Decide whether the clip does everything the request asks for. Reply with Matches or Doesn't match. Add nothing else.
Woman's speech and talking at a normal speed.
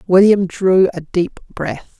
Matches